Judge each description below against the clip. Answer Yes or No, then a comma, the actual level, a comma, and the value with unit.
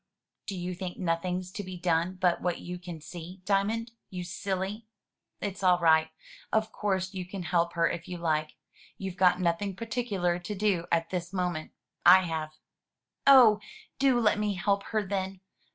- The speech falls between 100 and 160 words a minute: No, average, 170 wpm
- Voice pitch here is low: No, medium, 185 Hz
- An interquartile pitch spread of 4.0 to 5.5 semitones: No, narrow, 2.4 semitones